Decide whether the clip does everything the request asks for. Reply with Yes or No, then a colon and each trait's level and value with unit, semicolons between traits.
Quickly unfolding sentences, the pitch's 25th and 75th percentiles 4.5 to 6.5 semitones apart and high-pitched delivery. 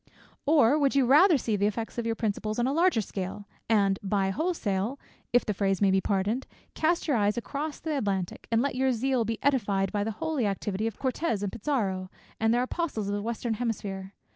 Yes: fast, 210 wpm; average, 4.9 semitones; high, 225 Hz